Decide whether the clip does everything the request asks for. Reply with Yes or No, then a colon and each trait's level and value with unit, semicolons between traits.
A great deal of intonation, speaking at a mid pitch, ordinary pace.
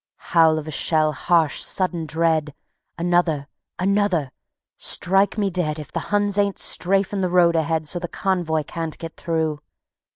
No: average, 2.9 semitones; medium, 170 Hz; average, 155 wpm